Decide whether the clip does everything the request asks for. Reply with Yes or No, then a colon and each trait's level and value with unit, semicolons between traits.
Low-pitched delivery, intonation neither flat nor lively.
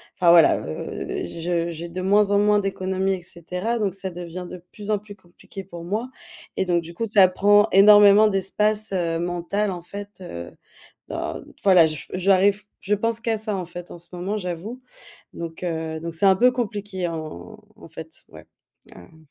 No: high, 190 Hz; average, 3.3 semitones